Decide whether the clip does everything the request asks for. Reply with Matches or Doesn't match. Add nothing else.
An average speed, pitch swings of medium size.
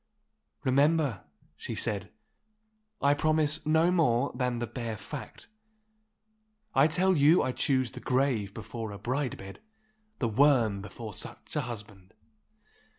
Doesn't match